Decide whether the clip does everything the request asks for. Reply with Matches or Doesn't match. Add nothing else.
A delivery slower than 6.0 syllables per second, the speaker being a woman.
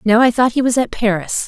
Matches